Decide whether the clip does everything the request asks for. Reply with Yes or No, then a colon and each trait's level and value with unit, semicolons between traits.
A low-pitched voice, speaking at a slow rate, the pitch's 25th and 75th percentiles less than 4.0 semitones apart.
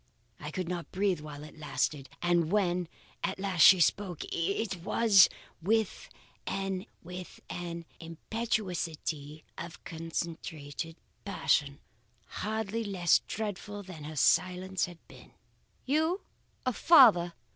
No: medium, 180 Hz; slow, 110 wpm; average, 3.6 semitones